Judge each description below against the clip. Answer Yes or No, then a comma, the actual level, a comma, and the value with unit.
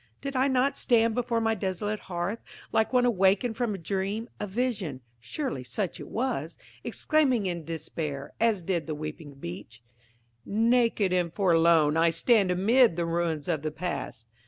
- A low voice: No, high, 190 Hz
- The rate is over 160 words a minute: No, average, 155 wpm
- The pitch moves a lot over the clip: Yes, wide, 6.1 semitones